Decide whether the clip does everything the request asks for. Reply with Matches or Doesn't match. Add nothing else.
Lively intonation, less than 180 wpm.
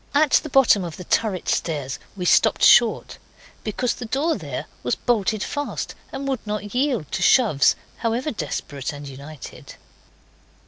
Matches